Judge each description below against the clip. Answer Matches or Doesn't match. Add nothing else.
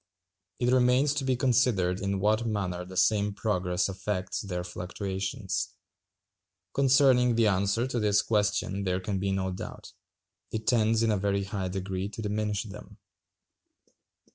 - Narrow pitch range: Doesn't match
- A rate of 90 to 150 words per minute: Matches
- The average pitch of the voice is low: Matches